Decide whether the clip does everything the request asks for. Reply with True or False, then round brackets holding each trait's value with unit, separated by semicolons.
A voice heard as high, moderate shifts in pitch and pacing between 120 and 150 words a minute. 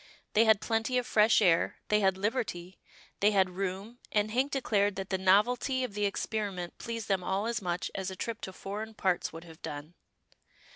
False (200 Hz; 3.0 semitones; 195 wpm)